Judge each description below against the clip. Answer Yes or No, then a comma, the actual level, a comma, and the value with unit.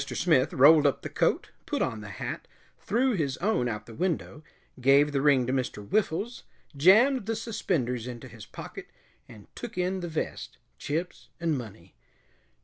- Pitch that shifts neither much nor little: No, wide, 6.9 semitones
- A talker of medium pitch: Yes, medium, 145 Hz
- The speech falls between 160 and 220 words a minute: Yes, average, 170 wpm